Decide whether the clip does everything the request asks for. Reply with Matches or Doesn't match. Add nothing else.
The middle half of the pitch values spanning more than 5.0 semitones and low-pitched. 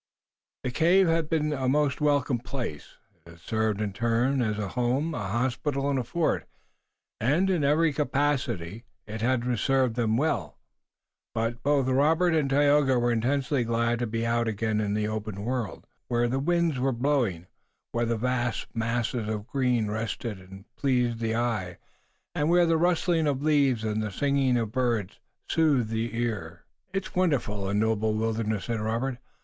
Doesn't match